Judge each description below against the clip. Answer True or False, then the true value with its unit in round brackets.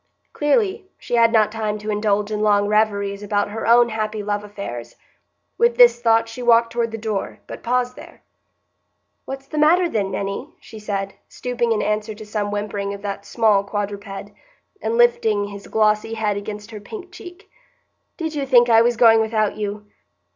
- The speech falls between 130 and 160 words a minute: False (180 wpm)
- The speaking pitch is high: True (215 Hz)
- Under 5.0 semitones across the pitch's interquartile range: True (2.5 semitones)